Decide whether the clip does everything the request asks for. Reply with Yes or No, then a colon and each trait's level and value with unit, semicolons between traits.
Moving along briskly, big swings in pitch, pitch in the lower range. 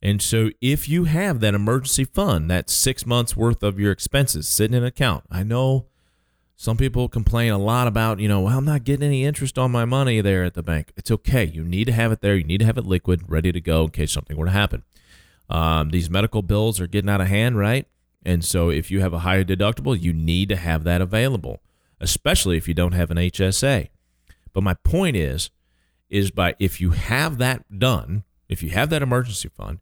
Yes: fast, 225 wpm; wide, 5.7 semitones; low, 100 Hz